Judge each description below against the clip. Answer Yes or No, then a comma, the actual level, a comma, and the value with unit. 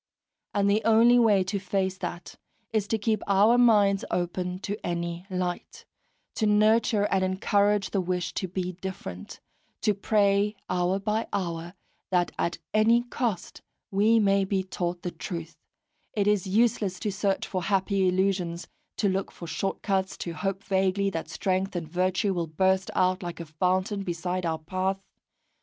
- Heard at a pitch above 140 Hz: Yes, high, 190 Hz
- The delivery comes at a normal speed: Yes, average, 160 wpm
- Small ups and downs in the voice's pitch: Yes, narrow, 2.3 semitones